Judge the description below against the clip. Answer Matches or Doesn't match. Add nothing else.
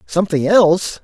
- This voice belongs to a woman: Doesn't match